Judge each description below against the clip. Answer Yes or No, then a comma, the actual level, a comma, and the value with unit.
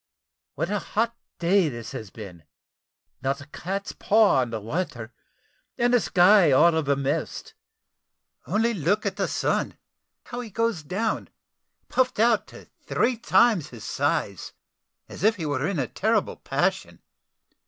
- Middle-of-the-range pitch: Yes, medium, 180 Hz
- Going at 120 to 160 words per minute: Yes, average, 155 wpm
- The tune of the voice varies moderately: No, wide, 7.7 semitones